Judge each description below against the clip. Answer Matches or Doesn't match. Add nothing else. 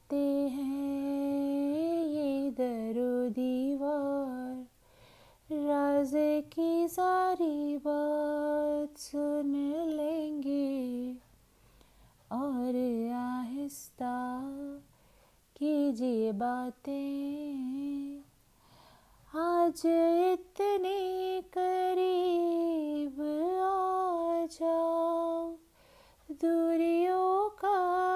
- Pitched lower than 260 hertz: Doesn't match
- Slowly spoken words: Matches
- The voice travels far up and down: Doesn't match